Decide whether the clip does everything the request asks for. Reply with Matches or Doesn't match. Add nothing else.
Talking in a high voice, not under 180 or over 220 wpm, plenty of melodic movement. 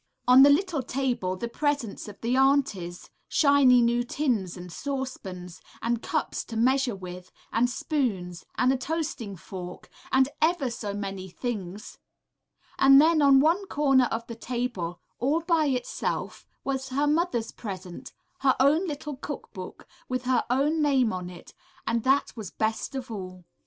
Doesn't match